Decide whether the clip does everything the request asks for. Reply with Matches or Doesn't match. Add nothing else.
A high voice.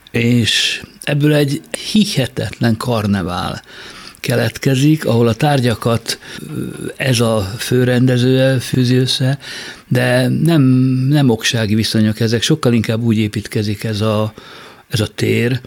Doesn't match